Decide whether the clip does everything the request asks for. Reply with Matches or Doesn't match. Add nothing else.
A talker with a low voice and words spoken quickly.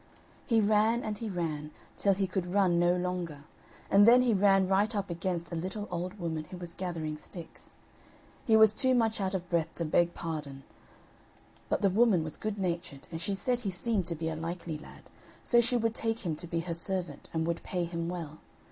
Doesn't match